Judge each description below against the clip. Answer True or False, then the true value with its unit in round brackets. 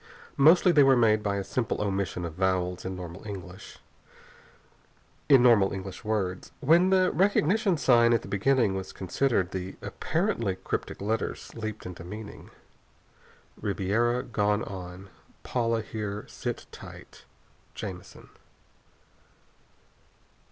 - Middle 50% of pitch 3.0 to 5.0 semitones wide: True (4.5 semitones)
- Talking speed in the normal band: False (115 wpm)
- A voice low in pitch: True (105 Hz)